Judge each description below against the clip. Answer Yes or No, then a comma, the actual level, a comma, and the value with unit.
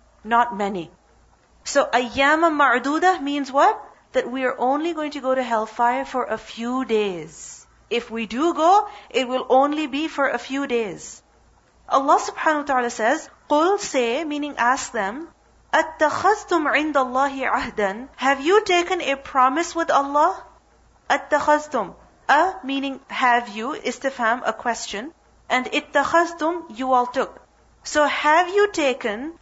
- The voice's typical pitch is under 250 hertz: No, very high, 275 Hz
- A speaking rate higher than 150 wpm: No, average, 145 wpm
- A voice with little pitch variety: No, average, 4.4 semitones